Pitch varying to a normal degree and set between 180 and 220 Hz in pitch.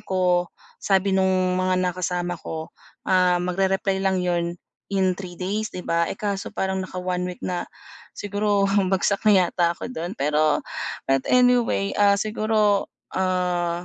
No: narrow, 2.0 semitones; medium, 185 Hz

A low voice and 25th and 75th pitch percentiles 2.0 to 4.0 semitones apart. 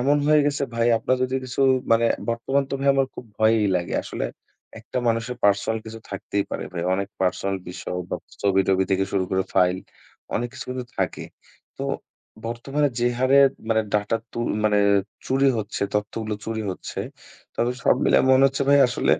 No: low, 115 Hz; average, 4.5 semitones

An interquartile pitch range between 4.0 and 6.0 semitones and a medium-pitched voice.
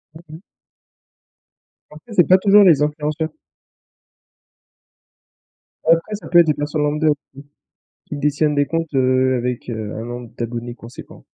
Yes: average, 4.6 semitones; medium, 150 Hz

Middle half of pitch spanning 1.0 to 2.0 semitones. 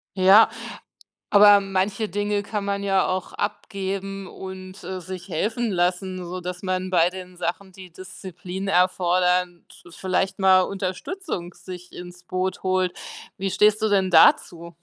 Yes: narrow, 1.6 semitones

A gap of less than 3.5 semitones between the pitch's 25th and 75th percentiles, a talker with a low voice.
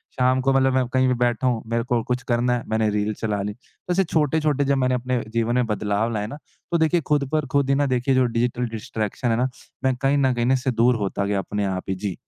Yes: average, 3.1 semitones; low, 125 Hz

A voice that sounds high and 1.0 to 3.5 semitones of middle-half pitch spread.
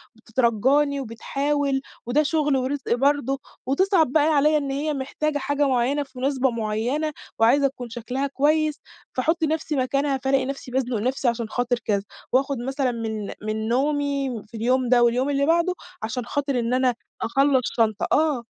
Yes: very high, 270 Hz; average, 3.0 semitones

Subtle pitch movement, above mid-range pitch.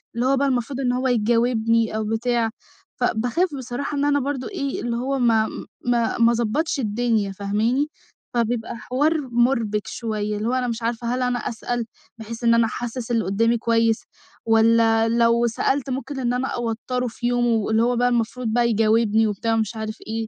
Yes: narrow, 1.8 semitones; high, 235 Hz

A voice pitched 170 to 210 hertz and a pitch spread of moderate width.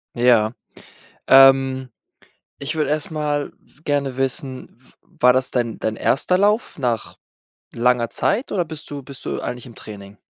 No: low, 135 Hz; average, 3.1 semitones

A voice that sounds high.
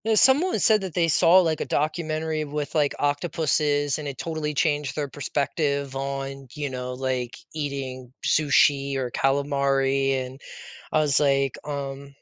No: medium, 145 Hz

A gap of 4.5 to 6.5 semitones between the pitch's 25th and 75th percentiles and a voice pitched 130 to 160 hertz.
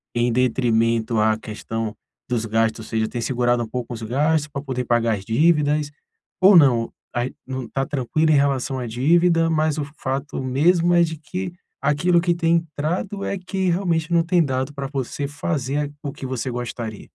Yes: average, 5.2 semitones; low, 135 Hz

